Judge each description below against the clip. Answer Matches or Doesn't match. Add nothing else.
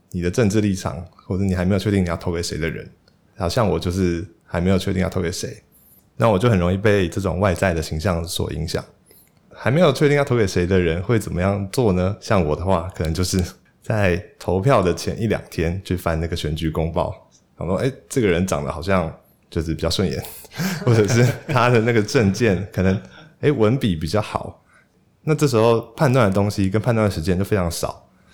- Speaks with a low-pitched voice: Matches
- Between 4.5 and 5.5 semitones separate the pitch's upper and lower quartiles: Doesn't match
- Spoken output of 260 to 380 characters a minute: Matches